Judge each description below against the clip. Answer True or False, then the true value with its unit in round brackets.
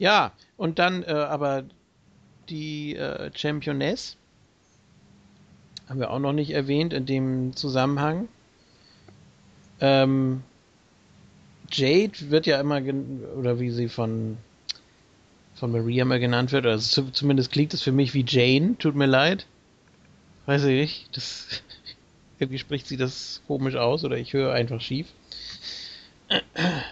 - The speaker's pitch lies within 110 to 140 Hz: True (135 Hz)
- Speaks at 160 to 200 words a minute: False (135 wpm)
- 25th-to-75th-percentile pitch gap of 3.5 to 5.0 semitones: False (2.8 semitones)